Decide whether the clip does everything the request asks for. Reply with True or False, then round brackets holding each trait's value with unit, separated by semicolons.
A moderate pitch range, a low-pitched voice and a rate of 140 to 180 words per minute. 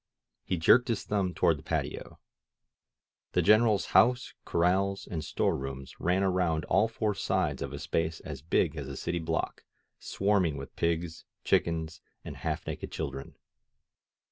True (3.9 semitones; 85 Hz; 150 wpm)